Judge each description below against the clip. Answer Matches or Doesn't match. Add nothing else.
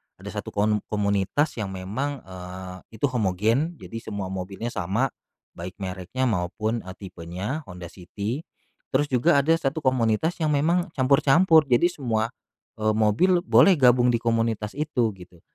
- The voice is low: Matches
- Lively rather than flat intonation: Matches